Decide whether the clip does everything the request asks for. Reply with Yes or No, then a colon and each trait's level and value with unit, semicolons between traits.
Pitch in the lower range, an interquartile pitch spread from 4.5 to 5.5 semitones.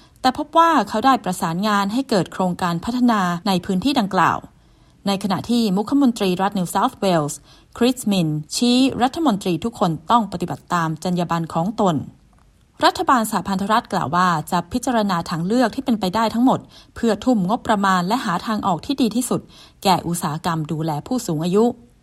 No: high, 200 Hz; average, 5.2 semitones